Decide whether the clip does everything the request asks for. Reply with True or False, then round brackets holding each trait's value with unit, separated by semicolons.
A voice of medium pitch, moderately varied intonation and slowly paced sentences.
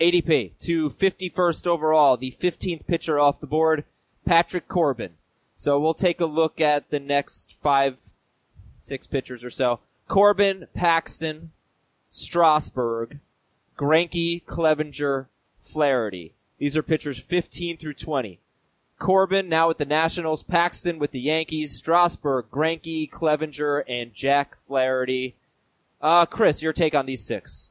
True (155 Hz; 3.3 semitones; 130 wpm)